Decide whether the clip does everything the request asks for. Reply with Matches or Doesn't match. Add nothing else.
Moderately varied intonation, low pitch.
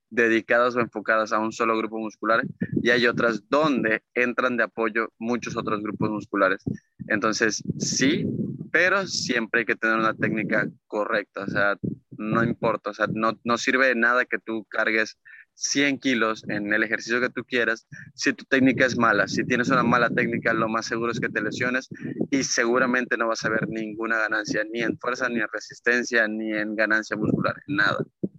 Doesn't match